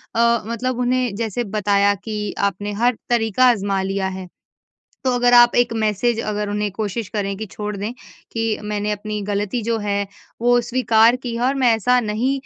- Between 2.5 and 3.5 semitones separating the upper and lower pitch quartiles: Yes, average, 2.8 semitones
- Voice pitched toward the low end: No, high, 220 Hz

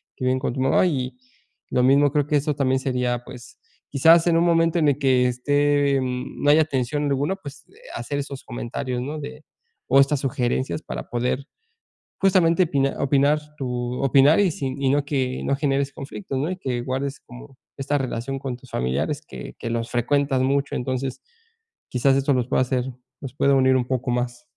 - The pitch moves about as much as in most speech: No, narrow, 2.3 semitones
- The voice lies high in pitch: No, low, 135 Hz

